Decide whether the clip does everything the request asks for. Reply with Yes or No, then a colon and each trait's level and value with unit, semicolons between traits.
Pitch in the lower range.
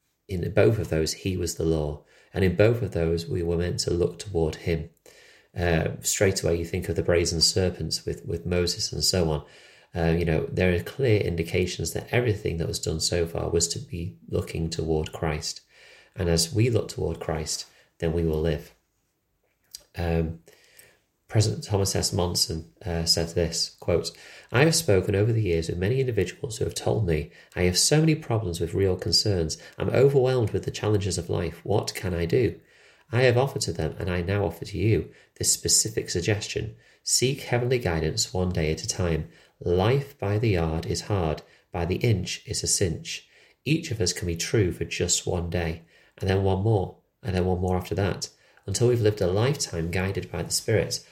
Yes: very low, 90 Hz